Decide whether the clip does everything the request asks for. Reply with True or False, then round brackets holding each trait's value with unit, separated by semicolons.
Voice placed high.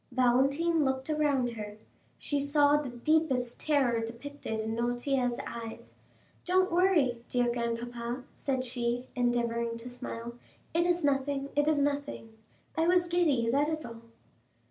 True (260 Hz)